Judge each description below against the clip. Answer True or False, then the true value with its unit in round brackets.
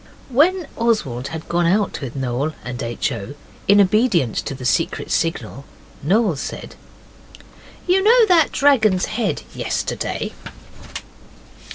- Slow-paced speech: True (125 wpm)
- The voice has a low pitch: False (185 Hz)